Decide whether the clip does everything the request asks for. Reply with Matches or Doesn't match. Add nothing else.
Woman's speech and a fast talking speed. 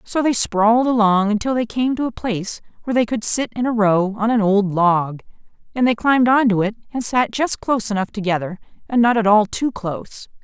Matches